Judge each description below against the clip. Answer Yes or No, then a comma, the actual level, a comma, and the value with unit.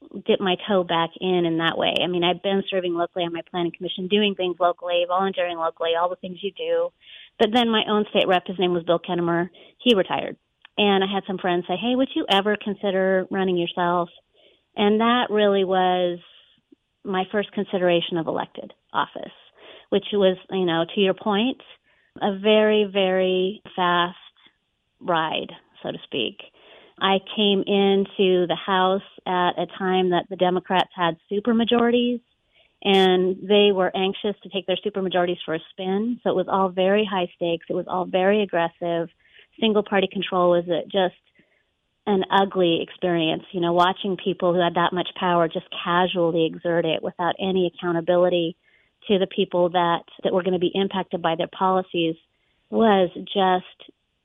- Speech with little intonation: Yes, narrow, 2.1 semitones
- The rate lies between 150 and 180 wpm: Yes, average, 175 wpm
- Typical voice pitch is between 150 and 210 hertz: Yes, medium, 185 Hz